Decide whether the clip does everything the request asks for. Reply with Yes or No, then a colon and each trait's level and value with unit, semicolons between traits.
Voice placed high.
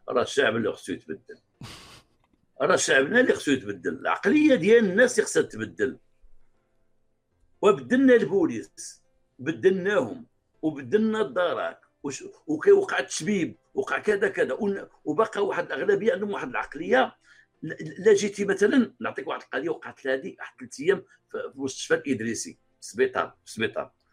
Yes: very high, 255 Hz